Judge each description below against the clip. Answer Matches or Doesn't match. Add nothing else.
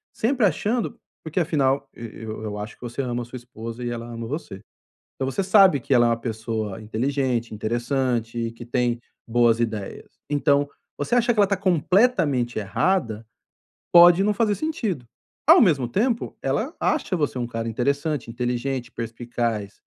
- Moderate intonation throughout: Doesn't match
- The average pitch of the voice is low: Matches